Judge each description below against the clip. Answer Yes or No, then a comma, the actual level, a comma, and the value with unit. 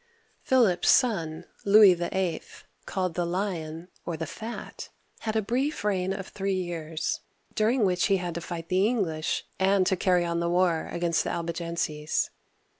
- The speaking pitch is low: No, medium, 180 Hz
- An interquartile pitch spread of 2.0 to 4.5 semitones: Yes, average, 2.8 semitones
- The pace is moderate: Yes, average, 160 wpm